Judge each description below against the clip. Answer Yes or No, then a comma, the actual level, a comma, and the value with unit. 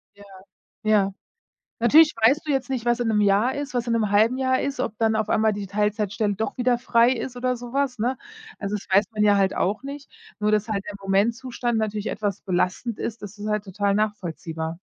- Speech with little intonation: No, average, 3.2 semitones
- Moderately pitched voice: No, high, 215 Hz